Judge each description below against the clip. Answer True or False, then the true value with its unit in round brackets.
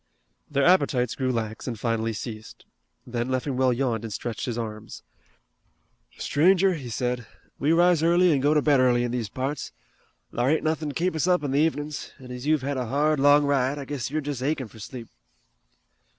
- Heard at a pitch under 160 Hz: True (135 Hz)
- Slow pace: False (195 wpm)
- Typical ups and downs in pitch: True (3.7 semitones)